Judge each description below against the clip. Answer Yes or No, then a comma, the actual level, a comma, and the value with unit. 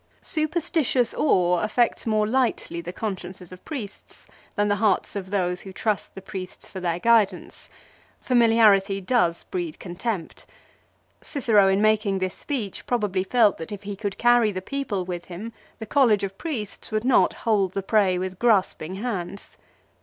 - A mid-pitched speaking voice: No, high, 205 Hz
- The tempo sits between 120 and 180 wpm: Yes, average, 160 wpm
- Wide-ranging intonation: No, average, 3.7 semitones